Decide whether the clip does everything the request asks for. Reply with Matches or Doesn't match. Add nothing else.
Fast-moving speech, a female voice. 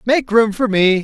Doesn't match